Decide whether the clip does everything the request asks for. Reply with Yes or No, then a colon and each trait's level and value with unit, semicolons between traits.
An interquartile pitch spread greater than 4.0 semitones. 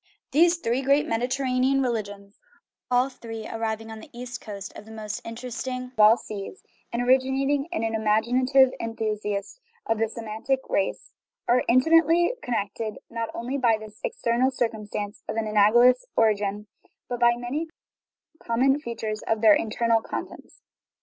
No: average, 2.8 semitones